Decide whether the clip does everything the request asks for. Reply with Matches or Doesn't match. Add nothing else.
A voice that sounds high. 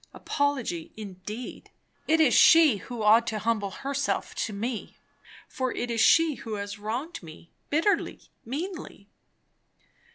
Matches